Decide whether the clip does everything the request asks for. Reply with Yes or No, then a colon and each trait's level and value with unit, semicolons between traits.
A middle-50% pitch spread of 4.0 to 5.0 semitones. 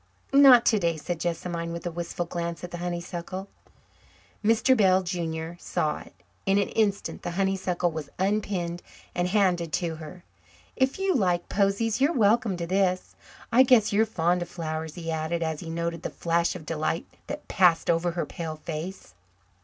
No: average, 2.9 semitones